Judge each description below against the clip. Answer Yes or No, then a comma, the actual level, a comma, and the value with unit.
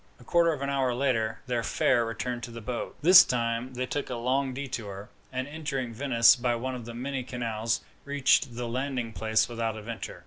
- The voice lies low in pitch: Yes, low, 125 Hz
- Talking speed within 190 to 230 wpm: Yes, average, 200 wpm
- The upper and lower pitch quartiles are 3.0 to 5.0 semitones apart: No, narrow, 2.5 semitones